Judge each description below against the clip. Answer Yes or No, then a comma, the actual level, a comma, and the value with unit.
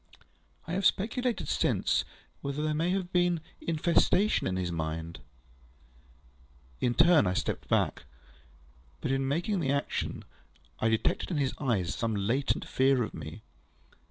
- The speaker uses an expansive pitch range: Yes, wide, 7.7 semitones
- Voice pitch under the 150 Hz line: Yes, medium, 140 Hz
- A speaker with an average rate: Yes, average, 145 wpm